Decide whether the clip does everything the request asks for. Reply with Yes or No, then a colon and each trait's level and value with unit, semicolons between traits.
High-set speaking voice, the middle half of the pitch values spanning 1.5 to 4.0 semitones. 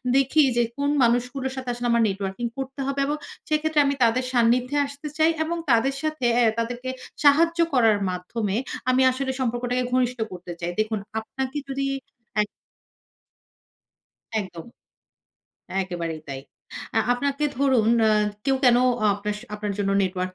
No: high, 245 Hz; average, 4.6 semitones